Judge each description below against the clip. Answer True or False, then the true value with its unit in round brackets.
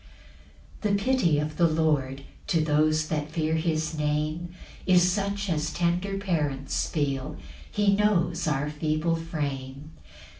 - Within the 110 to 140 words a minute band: True (135 wpm)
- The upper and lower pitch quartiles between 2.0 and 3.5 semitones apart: True (2.9 semitones)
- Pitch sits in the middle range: True (160 Hz)